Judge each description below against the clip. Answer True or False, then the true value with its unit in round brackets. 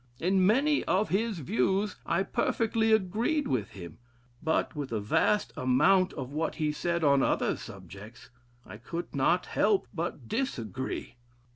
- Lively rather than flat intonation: True (8.2 semitones)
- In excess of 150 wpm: False (145 wpm)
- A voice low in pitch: False (170 Hz)